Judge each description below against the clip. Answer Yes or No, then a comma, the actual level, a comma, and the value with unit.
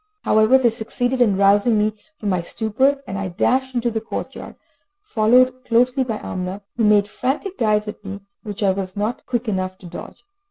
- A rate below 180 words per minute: No, average, 195 wpm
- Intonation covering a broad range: No, average, 3.8 semitones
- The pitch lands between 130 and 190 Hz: No, high, 220 Hz